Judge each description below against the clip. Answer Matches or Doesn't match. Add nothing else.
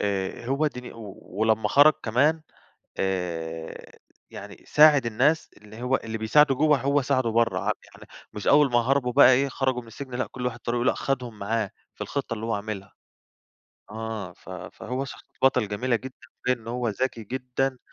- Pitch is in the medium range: Doesn't match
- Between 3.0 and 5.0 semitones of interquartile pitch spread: Matches